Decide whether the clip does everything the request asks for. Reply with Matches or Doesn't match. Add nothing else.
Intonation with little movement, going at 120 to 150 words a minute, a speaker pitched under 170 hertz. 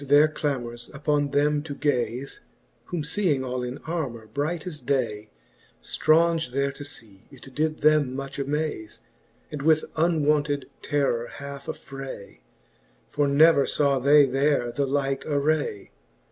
Matches